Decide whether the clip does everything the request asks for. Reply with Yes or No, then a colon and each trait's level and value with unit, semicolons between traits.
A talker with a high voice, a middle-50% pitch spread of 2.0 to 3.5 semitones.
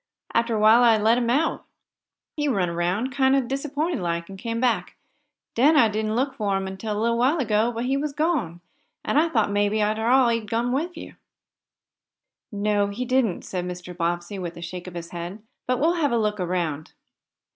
No: high, 220 Hz; average, 5.2 semitones